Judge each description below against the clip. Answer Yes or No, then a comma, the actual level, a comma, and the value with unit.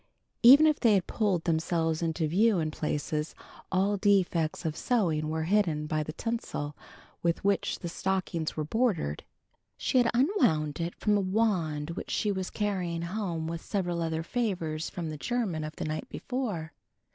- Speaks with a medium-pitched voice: Yes, medium, 170 Hz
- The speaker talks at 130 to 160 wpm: No, average, 170 wpm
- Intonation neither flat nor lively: Yes, average, 4.6 semitones